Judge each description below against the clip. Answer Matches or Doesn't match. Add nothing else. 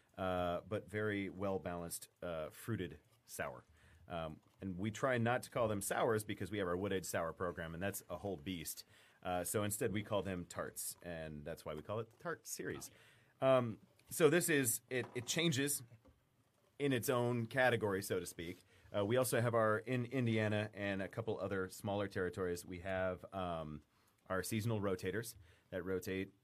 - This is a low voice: Matches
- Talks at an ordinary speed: Matches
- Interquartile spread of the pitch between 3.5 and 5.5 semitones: Matches